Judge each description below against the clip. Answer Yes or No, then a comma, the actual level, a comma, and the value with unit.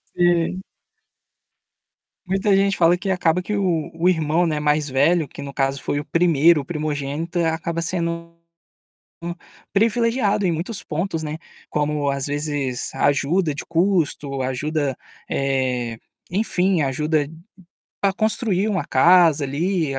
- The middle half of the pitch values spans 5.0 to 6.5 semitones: No, average, 3.9 semitones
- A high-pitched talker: No, medium, 165 Hz